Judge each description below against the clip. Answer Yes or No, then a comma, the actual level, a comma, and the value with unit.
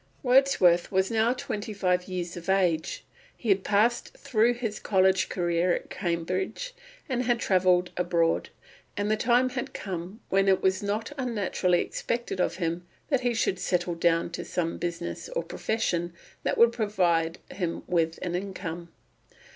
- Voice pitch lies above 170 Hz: Yes, high, 190 Hz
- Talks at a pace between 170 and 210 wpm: No, average, 155 wpm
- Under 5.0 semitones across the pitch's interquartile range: Yes, average, 4.4 semitones